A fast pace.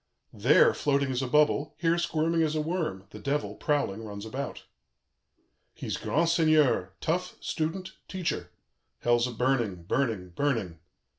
No: average, 140 wpm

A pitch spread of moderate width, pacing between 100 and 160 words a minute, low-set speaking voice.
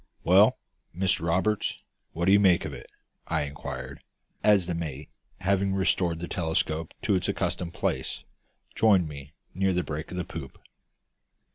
Yes: average, 3.6 semitones; average, 155 wpm; very low, 85 Hz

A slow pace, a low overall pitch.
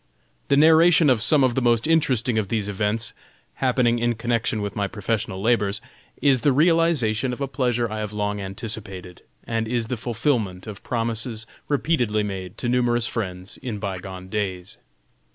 No: average, 170 wpm; low, 115 Hz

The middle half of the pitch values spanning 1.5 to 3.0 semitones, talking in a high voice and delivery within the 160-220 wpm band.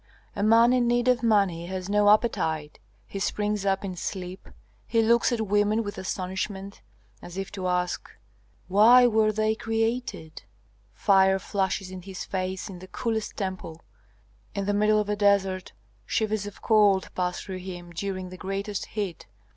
Yes: narrow, 2.4 semitones; high, 200 Hz; average, 165 wpm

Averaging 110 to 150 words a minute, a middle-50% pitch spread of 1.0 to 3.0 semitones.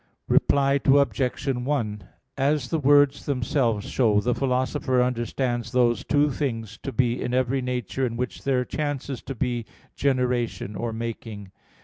Yes: average, 140 wpm; average, 2.7 semitones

